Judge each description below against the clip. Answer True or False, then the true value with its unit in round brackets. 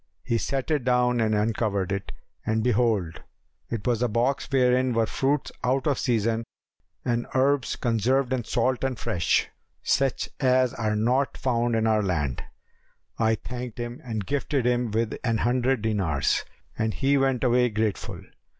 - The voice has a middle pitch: False (120 Hz)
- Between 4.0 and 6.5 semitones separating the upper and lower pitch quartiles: False (2.7 semitones)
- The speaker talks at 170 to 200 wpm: False (160 wpm)